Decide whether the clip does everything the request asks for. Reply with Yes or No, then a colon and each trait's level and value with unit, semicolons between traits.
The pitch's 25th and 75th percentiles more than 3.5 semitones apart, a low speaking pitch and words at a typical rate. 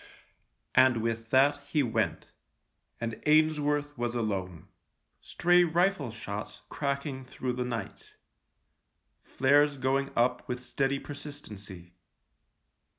No: average, 4.1 semitones; low, 130 Hz; slow, 110 wpm